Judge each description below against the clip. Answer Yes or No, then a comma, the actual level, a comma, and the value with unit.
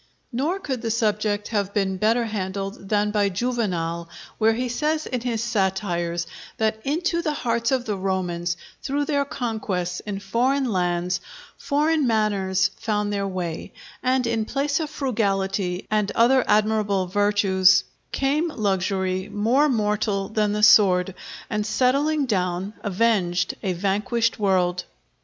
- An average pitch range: Yes, average, 4.1 semitones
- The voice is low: No, high, 210 Hz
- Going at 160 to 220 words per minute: No, average, 140 wpm